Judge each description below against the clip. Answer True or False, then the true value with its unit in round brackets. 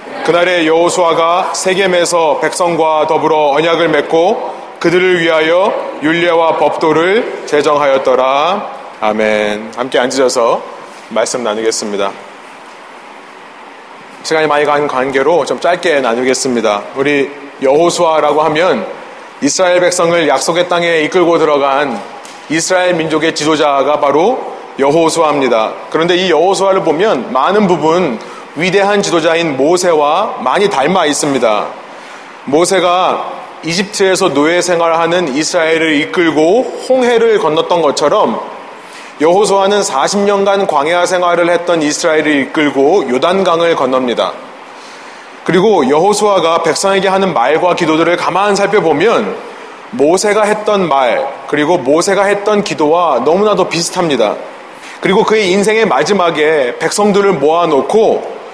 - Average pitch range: True (4.1 semitones)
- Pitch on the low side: False (170 Hz)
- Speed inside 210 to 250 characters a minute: False (295 characters per minute)